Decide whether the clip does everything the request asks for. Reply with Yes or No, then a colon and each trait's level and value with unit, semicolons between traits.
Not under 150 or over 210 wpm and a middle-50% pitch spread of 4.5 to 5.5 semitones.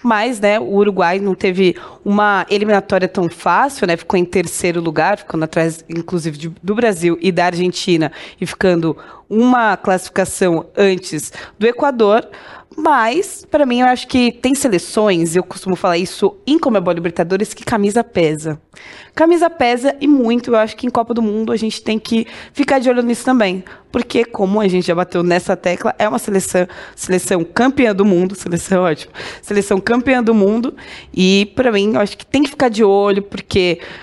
Yes: average, 180 wpm; average, 4.8 semitones